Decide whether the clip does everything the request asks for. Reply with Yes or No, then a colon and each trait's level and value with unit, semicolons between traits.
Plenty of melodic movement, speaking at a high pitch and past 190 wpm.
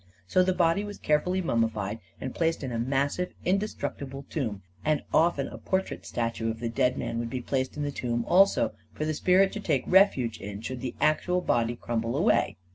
No: wide, 7.2 semitones; low, 135 Hz; average, 200 wpm